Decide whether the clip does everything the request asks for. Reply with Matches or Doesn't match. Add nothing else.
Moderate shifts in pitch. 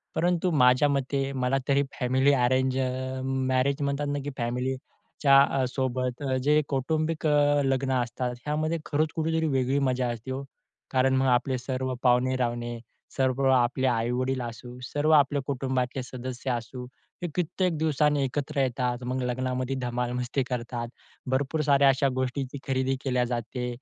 Doesn't match